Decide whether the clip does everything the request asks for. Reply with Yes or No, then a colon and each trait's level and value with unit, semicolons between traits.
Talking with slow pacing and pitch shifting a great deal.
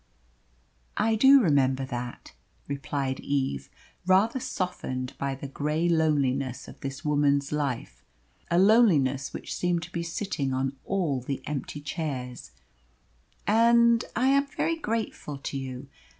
Yes: slow, 130 wpm; wide, 6.1 semitones